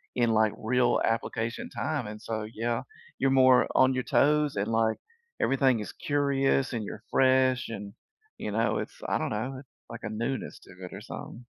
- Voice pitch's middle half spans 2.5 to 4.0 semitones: Yes, average, 3.2 semitones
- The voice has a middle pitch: No, low, 120 Hz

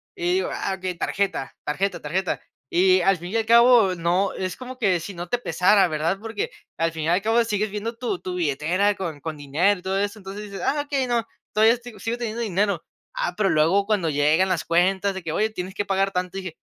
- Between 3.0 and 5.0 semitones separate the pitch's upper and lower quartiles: Yes, average, 3.6 semitones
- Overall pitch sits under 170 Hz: No, high, 195 Hz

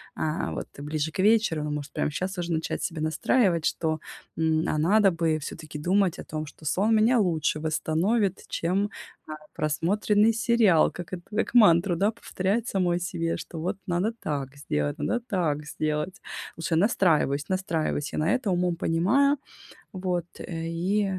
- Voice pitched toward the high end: No, medium, 175 Hz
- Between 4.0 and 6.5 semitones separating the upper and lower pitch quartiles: Yes, average, 4.3 semitones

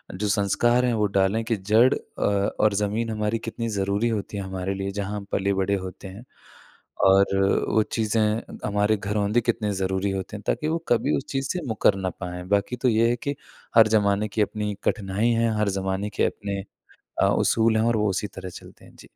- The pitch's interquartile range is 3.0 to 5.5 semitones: No, narrow, 2.5 semitones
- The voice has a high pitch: No, low, 105 Hz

